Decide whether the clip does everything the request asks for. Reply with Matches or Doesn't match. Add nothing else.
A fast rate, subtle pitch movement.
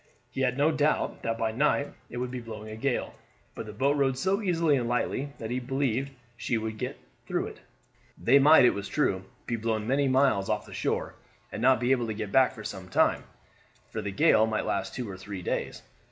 Doesn't match